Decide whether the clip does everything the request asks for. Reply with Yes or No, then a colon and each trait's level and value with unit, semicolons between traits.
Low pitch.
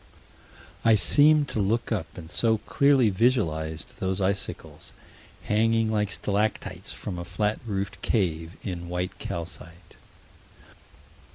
Yes: low, 100 Hz